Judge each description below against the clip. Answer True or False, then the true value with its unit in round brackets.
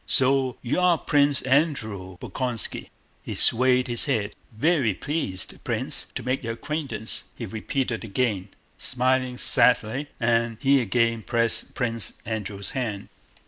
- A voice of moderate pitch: False (120 Hz)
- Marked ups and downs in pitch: False (3.3 semitones)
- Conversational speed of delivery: False (130 wpm)